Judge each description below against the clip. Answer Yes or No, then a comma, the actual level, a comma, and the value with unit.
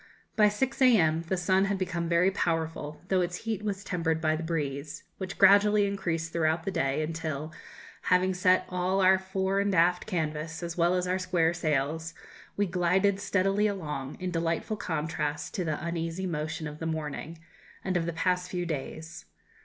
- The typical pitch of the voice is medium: Yes, medium, 170 Hz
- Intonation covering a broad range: No, average, 2.9 semitones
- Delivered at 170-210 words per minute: Yes, average, 175 wpm